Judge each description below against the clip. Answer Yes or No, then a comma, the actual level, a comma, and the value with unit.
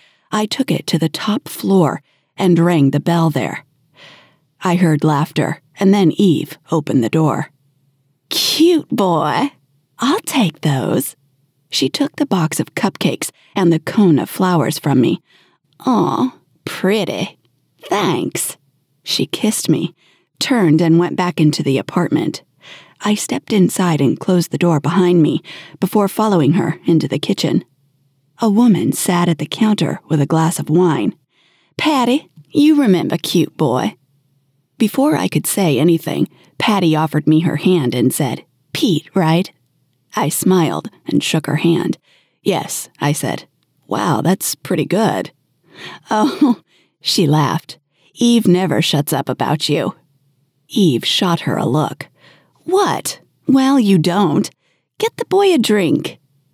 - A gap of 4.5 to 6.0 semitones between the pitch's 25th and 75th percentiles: Yes, average, 5.0 semitones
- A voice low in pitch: No, medium, 165 Hz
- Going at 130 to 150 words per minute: Yes, average, 140 wpm